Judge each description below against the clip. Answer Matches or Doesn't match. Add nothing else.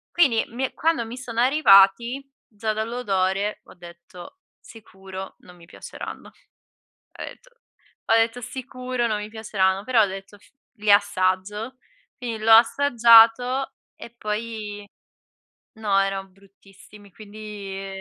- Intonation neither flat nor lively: Matches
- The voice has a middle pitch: Doesn't match